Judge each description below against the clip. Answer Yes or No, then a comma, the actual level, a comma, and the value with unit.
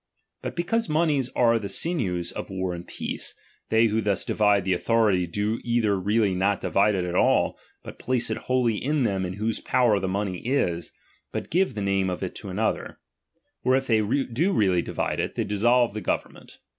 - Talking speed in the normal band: Yes, average, 195 wpm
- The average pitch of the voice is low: Yes, low, 105 Hz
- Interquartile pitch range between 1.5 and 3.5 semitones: No, average, 4.3 semitones